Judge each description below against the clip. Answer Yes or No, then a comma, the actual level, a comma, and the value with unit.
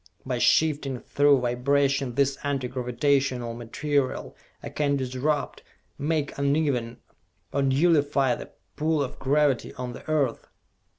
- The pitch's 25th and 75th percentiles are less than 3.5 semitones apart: Yes, narrow, 2.4 semitones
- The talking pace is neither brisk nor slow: No, slow, 120 wpm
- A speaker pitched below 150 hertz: Yes, medium, 140 Hz